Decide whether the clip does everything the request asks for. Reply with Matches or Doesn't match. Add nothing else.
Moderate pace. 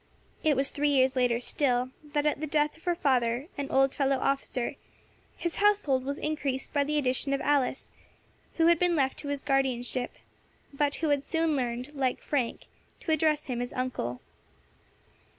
Matches